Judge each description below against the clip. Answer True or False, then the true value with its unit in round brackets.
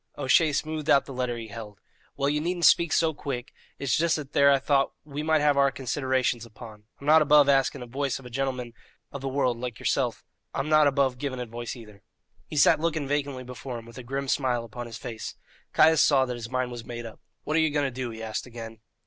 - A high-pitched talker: False (135 Hz)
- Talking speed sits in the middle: False (235 wpm)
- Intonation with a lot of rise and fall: False (3.2 semitones)